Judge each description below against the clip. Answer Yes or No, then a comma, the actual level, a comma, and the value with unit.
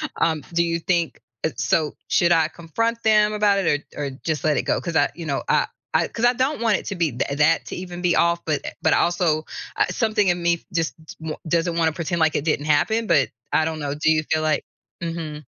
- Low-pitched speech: No, medium, 165 Hz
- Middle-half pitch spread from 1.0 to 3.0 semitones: Yes, narrow, 2.4 semitones